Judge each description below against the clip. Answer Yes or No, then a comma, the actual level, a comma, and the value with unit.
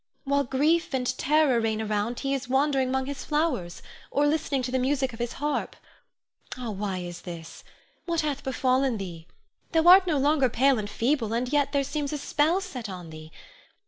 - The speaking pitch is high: Yes, very high, 265 Hz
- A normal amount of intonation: Yes, average, 4.6 semitones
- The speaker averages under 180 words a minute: No, average, 185 wpm